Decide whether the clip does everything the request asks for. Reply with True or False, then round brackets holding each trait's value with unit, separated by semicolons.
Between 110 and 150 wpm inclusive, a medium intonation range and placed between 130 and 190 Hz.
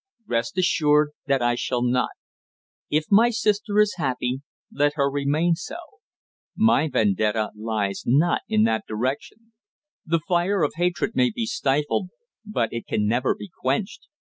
False (145 wpm; 6.4 semitones; 140 Hz)